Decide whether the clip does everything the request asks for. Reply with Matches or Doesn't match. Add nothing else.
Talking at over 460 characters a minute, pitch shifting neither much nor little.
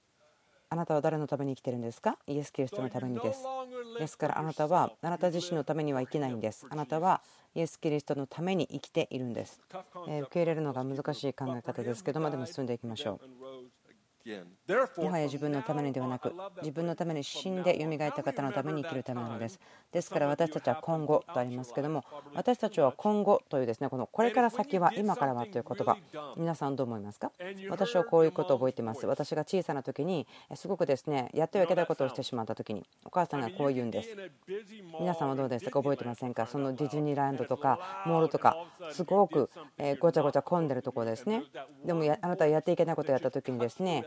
Matches